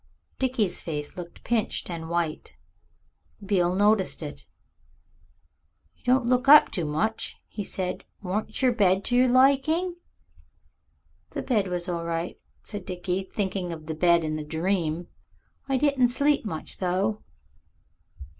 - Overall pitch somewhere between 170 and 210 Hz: Yes, high, 190 Hz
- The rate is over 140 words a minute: No, slow, 135 wpm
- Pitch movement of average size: No, wide, 6.1 semitones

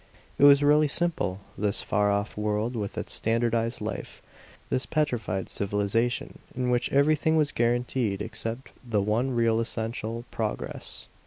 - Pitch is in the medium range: No, low, 115 Hz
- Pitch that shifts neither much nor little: Yes, average, 3.5 semitones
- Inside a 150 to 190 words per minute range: No, average, 140 wpm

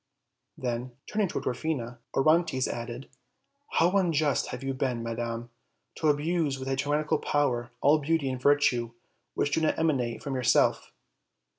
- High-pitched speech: No, low, 135 Hz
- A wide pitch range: No, average, 4.1 semitones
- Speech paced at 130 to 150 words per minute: Yes, average, 145 wpm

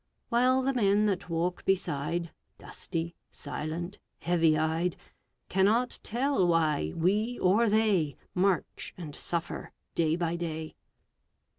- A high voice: No, medium, 175 Hz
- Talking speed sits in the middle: No, slow, 115 wpm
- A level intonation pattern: No, average, 4.2 semitones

